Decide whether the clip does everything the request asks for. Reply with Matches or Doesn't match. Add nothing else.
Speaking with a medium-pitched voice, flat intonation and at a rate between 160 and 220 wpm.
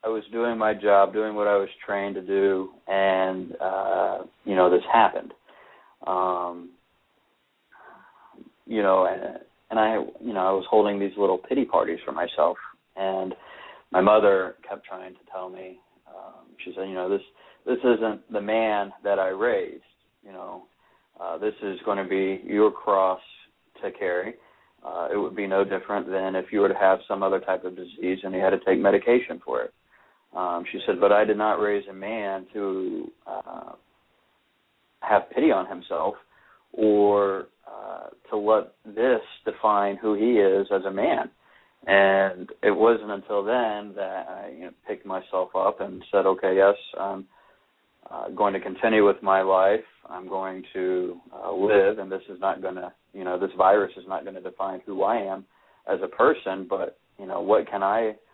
Doesn't match